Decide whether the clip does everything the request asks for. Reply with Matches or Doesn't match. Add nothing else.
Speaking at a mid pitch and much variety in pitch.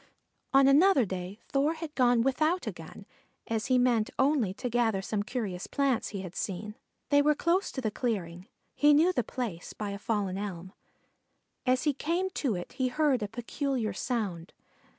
Doesn't match